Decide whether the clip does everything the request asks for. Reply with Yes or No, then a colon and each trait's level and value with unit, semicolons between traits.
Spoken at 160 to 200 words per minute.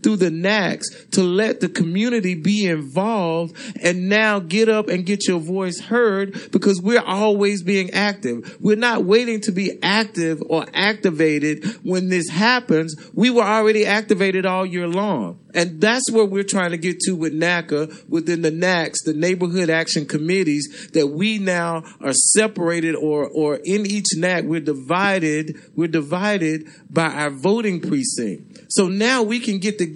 Yes: average, 165 wpm